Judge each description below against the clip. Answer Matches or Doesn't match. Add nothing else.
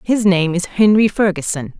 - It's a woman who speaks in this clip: Matches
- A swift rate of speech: Doesn't match